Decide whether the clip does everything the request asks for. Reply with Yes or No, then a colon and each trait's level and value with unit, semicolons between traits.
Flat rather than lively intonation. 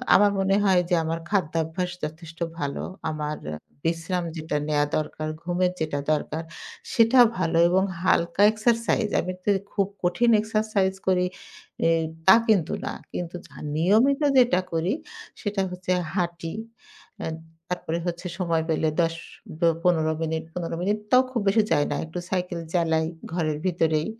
No: average, 3.3 semitones